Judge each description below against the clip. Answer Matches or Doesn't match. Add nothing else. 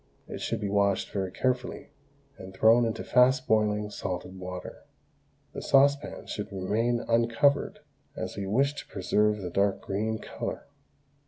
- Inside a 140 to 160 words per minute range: Matches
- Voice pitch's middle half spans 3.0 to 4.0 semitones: Matches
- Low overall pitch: Matches